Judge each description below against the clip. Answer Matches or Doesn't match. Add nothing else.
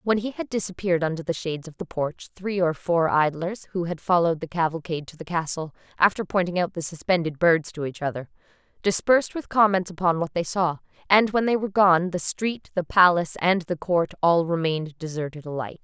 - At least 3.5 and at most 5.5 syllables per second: Doesn't match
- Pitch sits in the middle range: Matches